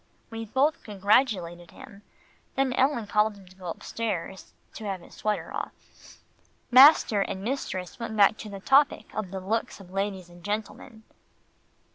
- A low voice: No, high, 210 Hz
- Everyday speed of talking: Yes, average, 155 wpm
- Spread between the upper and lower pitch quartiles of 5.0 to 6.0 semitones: No, average, 3.3 semitones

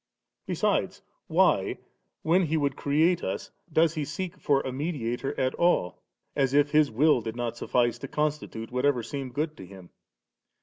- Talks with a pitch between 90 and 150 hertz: Yes, medium, 140 Hz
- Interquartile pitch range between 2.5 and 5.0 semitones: Yes, average, 4.1 semitones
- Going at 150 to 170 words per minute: Yes, average, 165 wpm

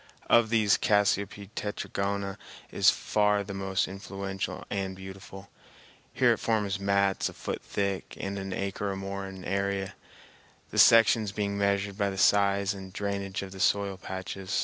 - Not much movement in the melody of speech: Yes, narrow, 0.7 semitones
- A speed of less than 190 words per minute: Yes, average, 155 wpm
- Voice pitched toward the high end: No, low, 100 Hz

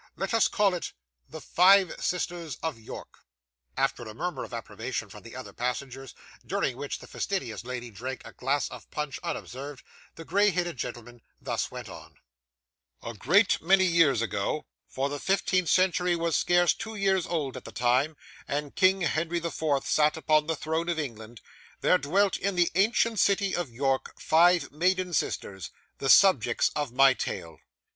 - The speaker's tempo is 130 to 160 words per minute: No, average, 170 wpm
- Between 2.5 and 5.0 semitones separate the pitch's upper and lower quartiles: No, wide, 5.6 semitones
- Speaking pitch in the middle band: Yes, medium, 160 Hz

